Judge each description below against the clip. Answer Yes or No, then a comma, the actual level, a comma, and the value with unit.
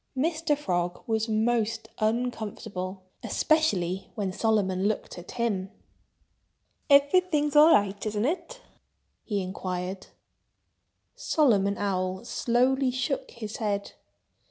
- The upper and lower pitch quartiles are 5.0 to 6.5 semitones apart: Yes, wide, 5.6 semitones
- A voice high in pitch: Yes, high, 220 Hz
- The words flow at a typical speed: No, slow, 95 wpm